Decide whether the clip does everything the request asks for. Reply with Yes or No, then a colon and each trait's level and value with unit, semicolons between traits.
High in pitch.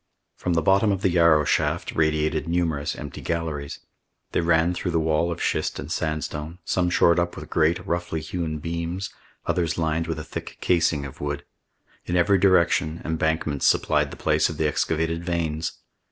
No: very low, 80 Hz